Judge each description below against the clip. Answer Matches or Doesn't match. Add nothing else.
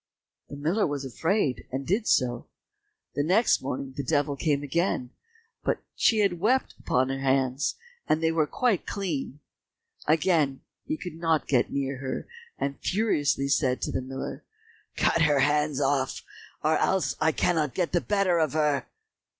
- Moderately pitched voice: Matches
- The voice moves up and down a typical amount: Matches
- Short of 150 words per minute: Doesn't match